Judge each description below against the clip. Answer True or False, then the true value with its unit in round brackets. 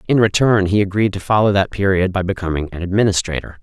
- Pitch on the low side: True (95 Hz)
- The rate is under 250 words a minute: True (200 wpm)